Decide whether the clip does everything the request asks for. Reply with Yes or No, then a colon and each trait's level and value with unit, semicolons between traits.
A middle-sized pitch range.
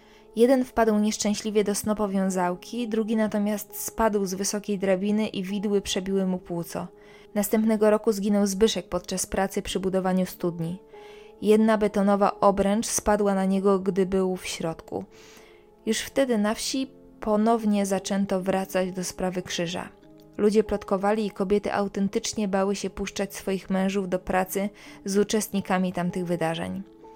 No: narrow, 2.0 semitones